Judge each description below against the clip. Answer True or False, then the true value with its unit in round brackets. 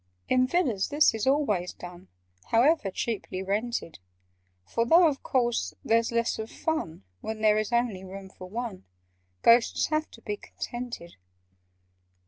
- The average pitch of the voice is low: False (230 Hz)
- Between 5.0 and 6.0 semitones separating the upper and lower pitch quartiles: False (4.2 semitones)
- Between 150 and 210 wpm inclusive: False (140 wpm)